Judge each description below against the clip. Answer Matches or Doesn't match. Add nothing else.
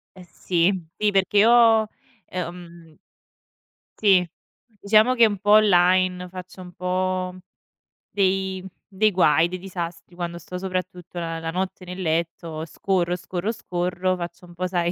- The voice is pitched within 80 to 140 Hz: Doesn't match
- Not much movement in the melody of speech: Matches